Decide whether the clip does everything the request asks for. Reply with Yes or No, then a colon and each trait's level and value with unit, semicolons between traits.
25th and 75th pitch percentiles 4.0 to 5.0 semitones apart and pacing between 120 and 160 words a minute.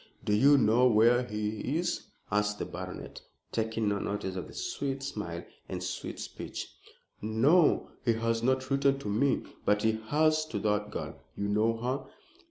No: average, 4.6 semitones; average, 170 wpm